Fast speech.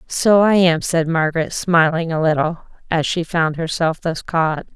No: average, 175 wpm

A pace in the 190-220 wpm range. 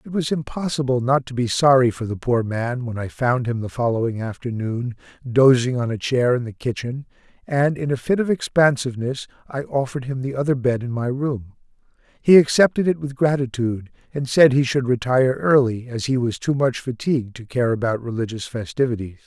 Yes: average, 195 wpm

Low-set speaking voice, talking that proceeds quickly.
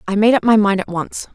No: high, 205 Hz; fast, 315 wpm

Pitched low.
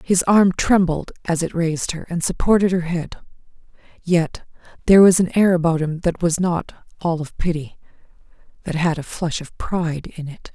No: medium, 170 Hz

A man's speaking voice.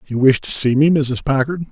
Yes: male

